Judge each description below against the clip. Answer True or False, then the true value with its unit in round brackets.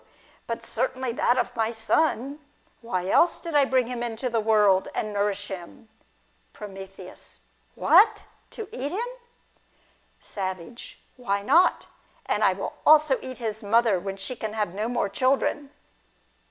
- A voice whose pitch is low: False (230 Hz)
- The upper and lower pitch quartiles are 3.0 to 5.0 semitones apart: True (4.3 semitones)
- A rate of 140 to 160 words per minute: True (145 wpm)